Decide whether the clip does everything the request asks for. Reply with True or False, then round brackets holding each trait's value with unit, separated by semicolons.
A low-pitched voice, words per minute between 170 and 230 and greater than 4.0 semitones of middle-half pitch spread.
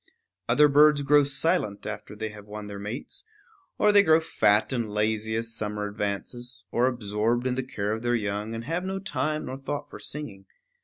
True (115 Hz; 195 wpm; 5.5 semitones)